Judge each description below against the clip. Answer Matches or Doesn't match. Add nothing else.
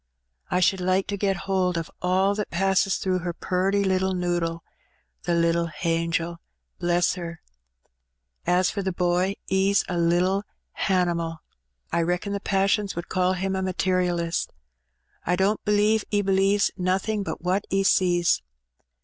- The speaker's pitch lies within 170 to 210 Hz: Matches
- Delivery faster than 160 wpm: Doesn't match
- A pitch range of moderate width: Doesn't match